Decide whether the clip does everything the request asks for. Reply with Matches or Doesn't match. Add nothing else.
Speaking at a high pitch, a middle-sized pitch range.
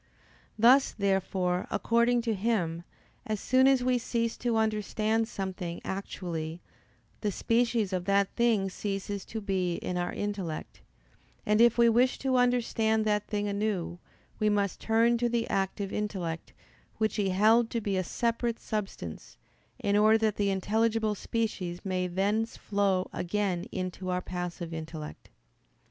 Matches